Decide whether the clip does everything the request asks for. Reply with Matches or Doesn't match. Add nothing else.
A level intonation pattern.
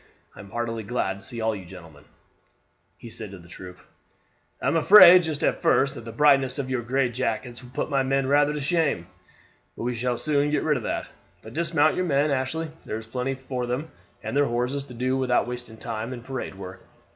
Doesn't match